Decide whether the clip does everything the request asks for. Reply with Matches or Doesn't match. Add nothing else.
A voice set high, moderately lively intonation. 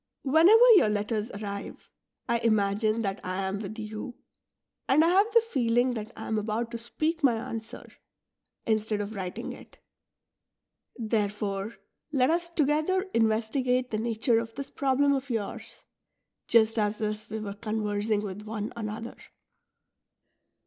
Matches